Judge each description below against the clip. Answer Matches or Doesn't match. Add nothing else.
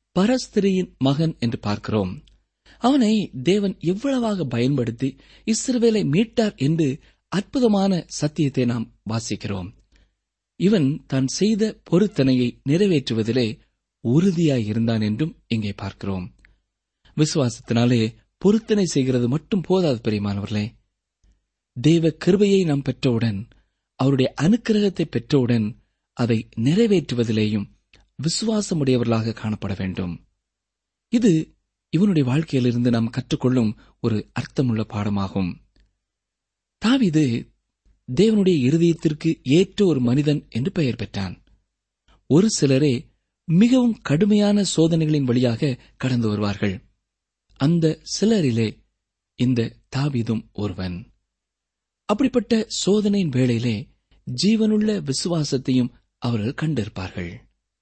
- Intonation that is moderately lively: Doesn't match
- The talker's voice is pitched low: Matches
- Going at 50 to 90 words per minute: Matches